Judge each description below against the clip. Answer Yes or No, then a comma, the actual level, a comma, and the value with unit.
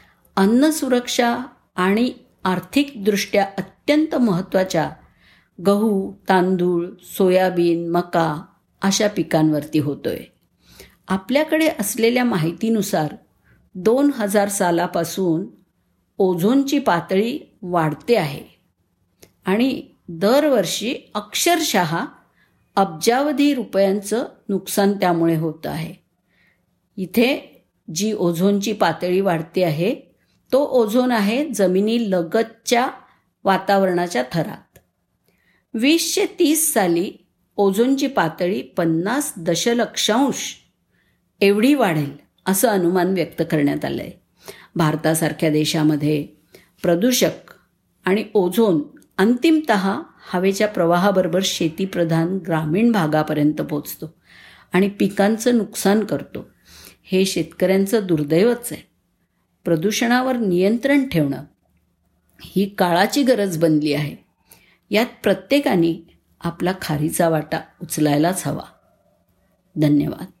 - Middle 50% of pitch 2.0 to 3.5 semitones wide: No, average, 5.3 semitones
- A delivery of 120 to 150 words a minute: No, slow, 80 wpm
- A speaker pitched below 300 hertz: Yes, high, 190 Hz